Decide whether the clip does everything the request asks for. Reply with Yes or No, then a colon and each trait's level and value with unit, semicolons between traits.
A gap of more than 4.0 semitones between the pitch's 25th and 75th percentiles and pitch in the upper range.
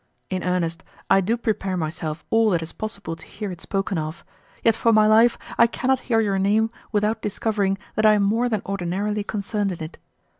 No: average, 3.3 semitones; high, 205 Hz